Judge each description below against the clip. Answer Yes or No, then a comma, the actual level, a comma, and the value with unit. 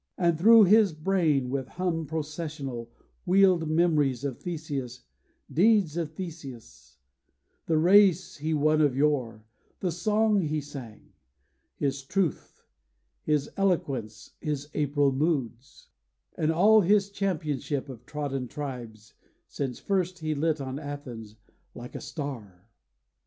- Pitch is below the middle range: No, medium, 150 Hz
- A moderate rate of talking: No, slow, 120 wpm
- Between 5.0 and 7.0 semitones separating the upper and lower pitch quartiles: No, average, 4.5 semitones